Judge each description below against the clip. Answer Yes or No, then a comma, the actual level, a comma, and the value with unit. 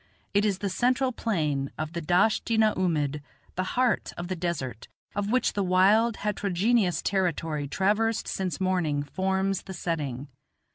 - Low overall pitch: No, medium, 185 Hz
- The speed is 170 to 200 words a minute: No, average, 155 wpm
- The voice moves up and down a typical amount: Yes, average, 4.2 semitones